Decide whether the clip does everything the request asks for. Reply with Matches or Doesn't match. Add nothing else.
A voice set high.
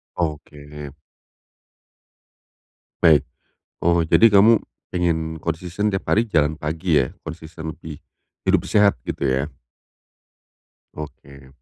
Doesn't match